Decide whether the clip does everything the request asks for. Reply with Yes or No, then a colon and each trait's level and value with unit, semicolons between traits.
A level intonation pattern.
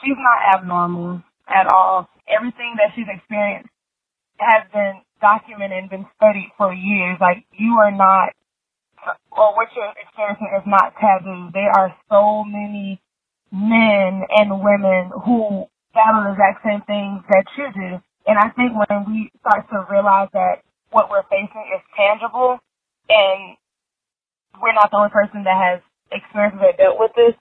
Yes: narrow, 2.1 semitones